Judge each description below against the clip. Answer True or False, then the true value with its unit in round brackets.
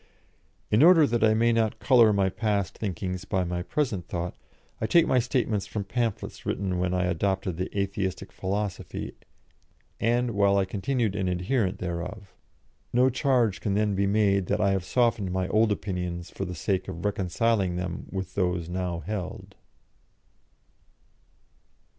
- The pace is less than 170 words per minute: True (155 wpm)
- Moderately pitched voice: False (100 Hz)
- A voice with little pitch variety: False (3.3 semitones)